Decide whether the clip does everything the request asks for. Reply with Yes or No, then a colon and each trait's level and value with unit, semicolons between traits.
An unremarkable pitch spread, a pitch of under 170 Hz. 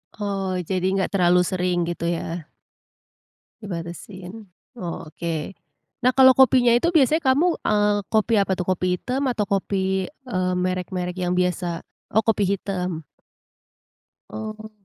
No: average, 3.3 semitones; high, 190 Hz